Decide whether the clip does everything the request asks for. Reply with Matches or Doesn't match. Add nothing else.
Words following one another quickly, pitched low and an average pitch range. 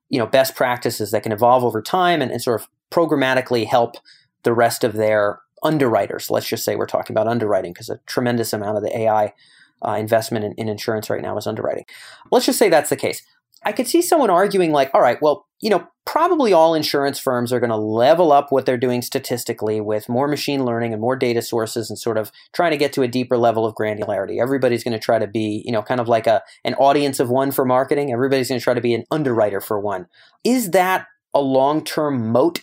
Matches